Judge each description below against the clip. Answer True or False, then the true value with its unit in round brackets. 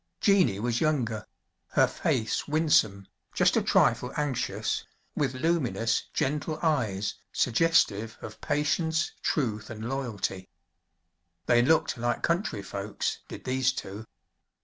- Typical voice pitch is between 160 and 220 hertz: False (125 Hz)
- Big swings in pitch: True (5.8 semitones)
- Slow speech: True (115 wpm)